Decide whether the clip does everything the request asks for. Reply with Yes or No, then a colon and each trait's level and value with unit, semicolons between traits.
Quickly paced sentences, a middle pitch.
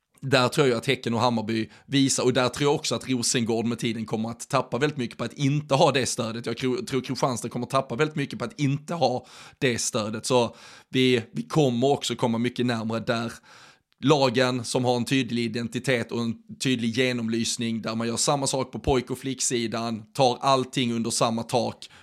No: fast, 205 wpm; low, 125 Hz